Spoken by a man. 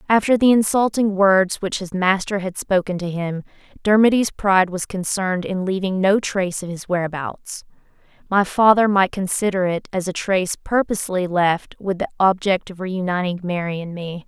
No: female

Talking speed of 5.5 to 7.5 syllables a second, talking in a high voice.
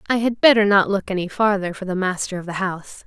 Yes: 6.2 syllables/s; high, 195 Hz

